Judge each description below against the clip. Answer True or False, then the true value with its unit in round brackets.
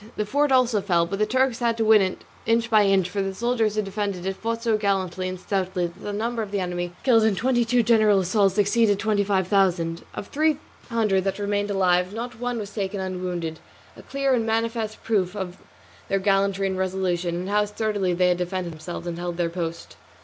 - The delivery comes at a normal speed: False (215 wpm)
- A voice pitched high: True (200 Hz)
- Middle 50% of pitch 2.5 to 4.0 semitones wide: True (3.3 semitones)